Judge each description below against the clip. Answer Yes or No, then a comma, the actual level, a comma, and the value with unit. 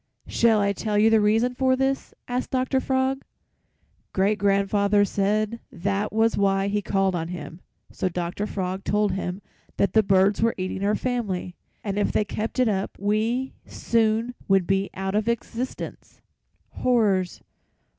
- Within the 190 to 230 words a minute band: No, average, 155 wpm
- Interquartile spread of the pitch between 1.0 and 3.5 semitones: Yes, average, 2.8 semitones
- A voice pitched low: No, high, 205 Hz